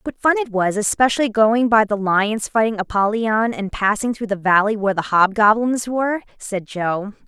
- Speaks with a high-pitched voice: Yes, high, 215 Hz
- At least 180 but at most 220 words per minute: Yes, average, 190 wpm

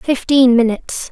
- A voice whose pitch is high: Yes, very high, 250 Hz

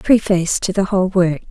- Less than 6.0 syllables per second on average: No, 6.1 syllables/s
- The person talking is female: Yes, female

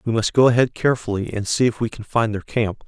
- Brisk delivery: Yes, fast, 270 wpm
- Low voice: Yes, low, 115 Hz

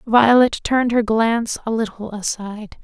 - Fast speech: No, average, 150 wpm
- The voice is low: No, high, 225 Hz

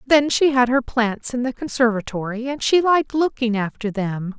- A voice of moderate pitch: No, high, 245 Hz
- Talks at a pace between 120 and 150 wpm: No, average, 190 wpm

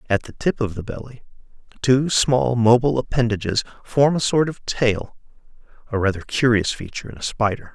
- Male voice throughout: Yes, male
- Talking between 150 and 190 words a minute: Yes, average, 170 wpm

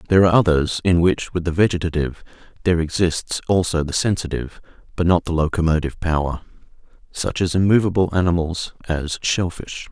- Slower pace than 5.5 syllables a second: No, 6.0 syllables/s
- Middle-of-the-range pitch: No, very low, 85 Hz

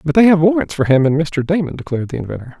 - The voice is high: No, medium, 155 Hz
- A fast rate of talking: Yes, fast, 275 wpm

